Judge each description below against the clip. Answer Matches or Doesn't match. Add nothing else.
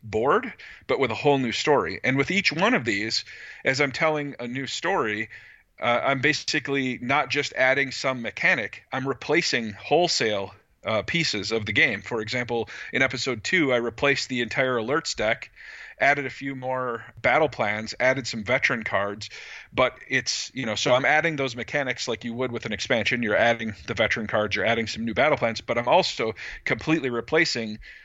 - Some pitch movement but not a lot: Matches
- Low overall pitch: Matches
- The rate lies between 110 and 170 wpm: Doesn't match